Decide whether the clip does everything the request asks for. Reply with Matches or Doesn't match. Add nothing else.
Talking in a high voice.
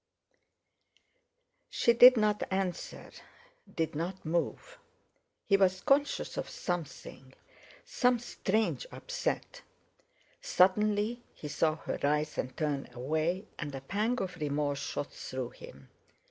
Doesn't match